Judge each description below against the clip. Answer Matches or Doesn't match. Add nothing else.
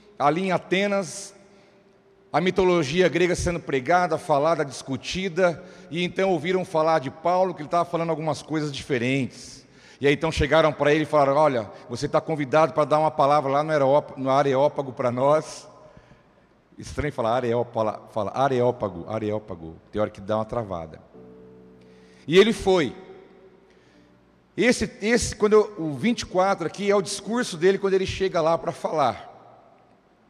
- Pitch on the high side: Doesn't match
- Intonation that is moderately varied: Doesn't match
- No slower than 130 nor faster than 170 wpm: Matches